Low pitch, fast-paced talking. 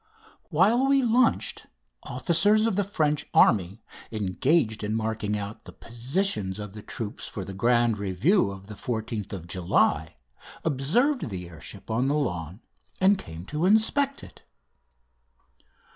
No: low, 115 Hz; average, 145 wpm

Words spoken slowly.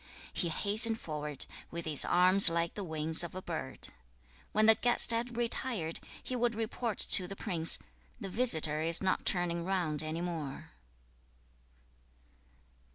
No: average, 155 wpm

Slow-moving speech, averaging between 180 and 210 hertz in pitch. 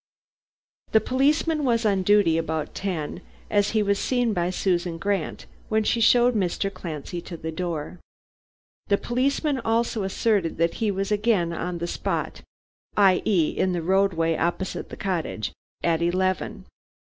No: average, 150 wpm; high, 190 Hz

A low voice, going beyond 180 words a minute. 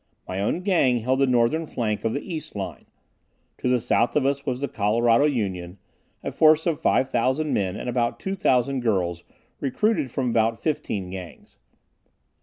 No: low, 125 Hz; average, 165 wpm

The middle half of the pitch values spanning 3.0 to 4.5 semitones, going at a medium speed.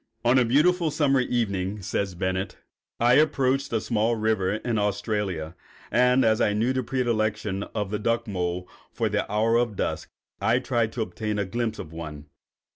Yes: average, 3.4 semitones; average, 180 wpm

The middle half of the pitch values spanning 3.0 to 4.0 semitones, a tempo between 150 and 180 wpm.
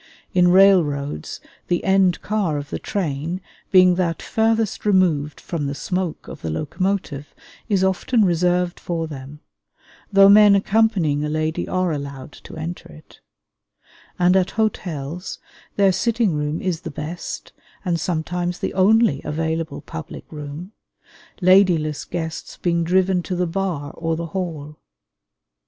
No: average, 3.7 semitones; average, 140 wpm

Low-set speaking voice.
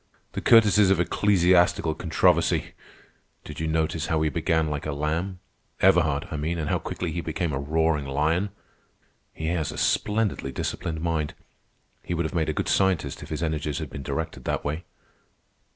Yes: very low, 80 Hz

